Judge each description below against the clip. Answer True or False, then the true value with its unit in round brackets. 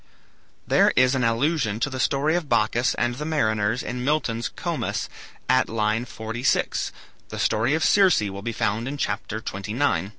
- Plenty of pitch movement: False (4.2 semitones)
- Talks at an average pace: True (165 wpm)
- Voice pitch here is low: True (120 Hz)